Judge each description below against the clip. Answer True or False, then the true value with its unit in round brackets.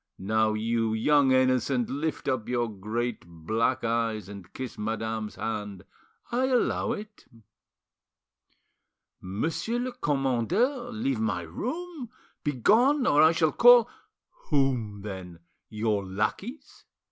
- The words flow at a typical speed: False (110 wpm)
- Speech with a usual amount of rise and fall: False (7.7 semitones)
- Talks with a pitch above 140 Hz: False (120 Hz)